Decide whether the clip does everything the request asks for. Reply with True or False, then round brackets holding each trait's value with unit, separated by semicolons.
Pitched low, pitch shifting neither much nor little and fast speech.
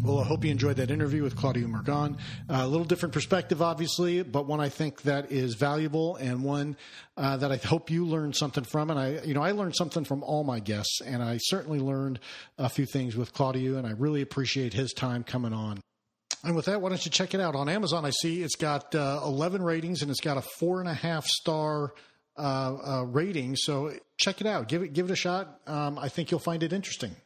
False (145 Hz; 3.8 semitones; 240 wpm)